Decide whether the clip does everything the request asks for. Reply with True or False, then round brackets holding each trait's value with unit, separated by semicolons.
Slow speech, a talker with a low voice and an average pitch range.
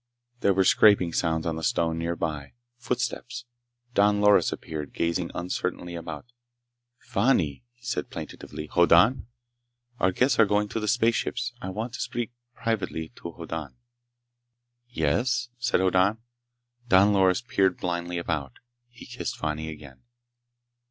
False (130 wpm; 95 Hz; 5.9 semitones)